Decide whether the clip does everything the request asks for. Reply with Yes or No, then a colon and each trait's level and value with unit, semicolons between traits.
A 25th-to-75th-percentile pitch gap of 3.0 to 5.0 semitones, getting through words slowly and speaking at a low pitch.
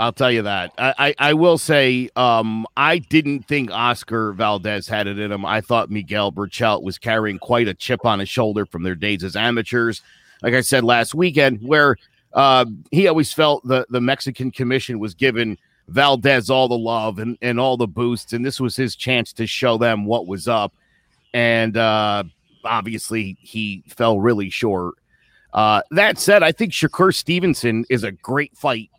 No: average, 3.6 semitones; average, 185 wpm; low, 120 Hz